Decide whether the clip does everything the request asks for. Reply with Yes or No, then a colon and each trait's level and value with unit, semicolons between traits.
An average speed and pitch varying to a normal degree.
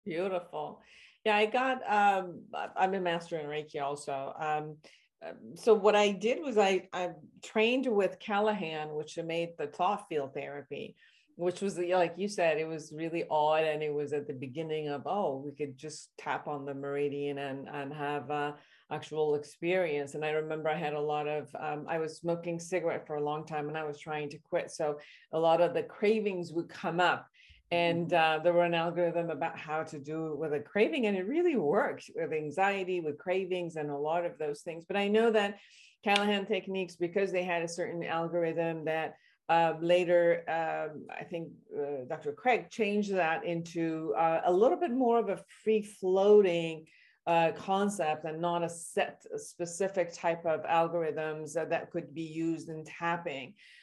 Yes: average, 190 wpm; average, 3.3 semitones